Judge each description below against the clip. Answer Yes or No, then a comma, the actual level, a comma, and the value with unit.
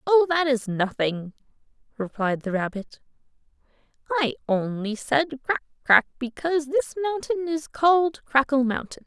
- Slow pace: Yes, slow, 125 wpm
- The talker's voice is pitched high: Yes, very high, 270 Hz